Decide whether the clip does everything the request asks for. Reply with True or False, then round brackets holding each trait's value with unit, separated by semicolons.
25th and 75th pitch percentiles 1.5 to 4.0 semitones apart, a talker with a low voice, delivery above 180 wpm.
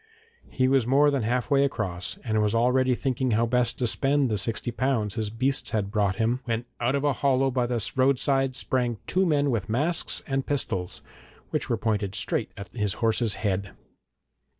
True (3.6 semitones; 120 Hz; 190 wpm)